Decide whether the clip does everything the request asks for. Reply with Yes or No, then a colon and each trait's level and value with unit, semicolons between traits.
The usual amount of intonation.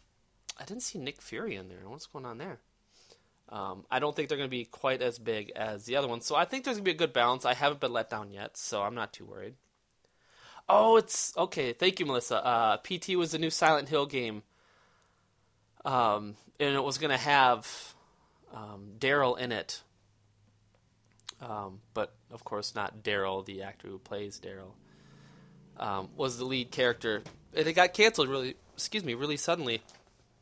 No: wide, 6.1 semitones